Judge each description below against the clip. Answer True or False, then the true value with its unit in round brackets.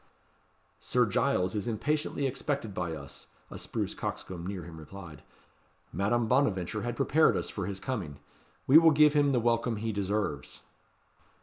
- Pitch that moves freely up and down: True (6.5 semitones)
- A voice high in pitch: False (110 Hz)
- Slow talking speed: False (150 wpm)